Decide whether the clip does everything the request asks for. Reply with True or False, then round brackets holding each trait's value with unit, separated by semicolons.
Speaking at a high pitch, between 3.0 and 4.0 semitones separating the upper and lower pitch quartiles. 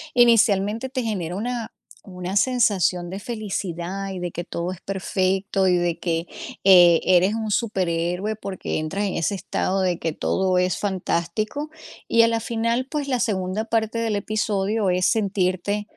True (195 Hz; 3.4 semitones)